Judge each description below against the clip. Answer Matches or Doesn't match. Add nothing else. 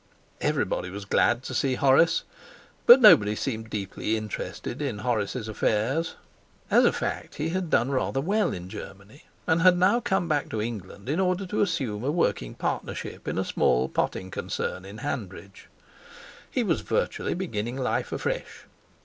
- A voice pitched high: Doesn't match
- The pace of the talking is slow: Doesn't match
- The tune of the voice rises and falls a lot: Matches